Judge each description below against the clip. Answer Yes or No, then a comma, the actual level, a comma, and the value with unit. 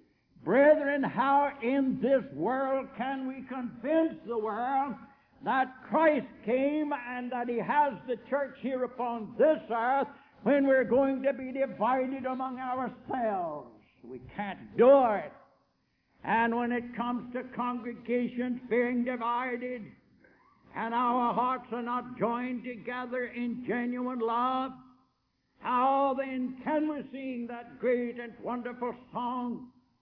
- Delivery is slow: Yes, slow, 125 wpm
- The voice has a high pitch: Yes, very high, 250 Hz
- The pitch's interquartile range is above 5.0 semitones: No, narrow, 1.8 semitones